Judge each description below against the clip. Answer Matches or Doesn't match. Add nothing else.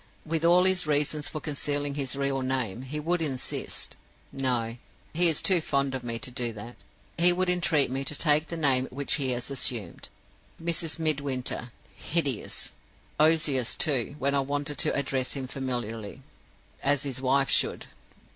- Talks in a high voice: Doesn't match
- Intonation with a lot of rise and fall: Doesn't match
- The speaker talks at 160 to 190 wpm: Matches